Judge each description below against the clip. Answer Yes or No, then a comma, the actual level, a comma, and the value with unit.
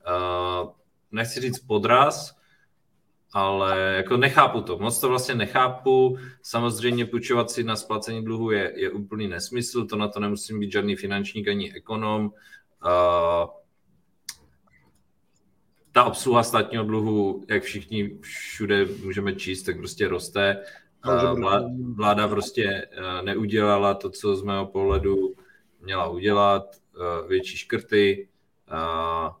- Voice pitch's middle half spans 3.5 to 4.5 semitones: No, average, 2.8 semitones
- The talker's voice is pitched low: Yes, low, 105 Hz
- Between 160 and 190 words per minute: No, average, 125 wpm